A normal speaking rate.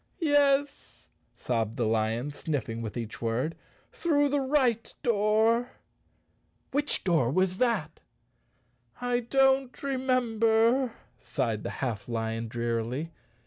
No: slow, 105 wpm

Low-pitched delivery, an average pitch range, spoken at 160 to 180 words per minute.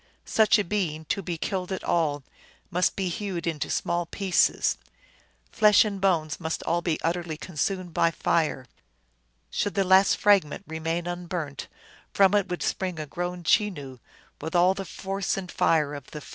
No: medium, 175 Hz; average, 3.2 semitones; average, 170 wpm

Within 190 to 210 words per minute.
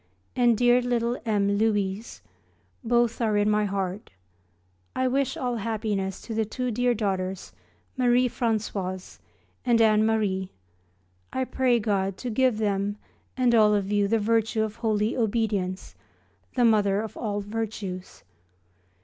No: average, 140 wpm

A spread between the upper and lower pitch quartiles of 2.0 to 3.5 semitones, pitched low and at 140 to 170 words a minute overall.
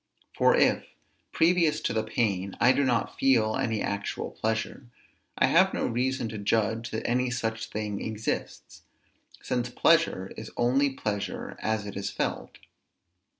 Yes: average, 3.1 semitones; low, 110 Hz; average, 150 wpm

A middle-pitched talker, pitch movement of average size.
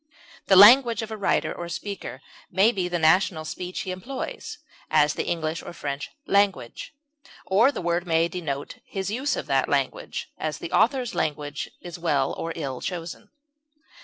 Yes: medium, 180 Hz; average, 4.2 semitones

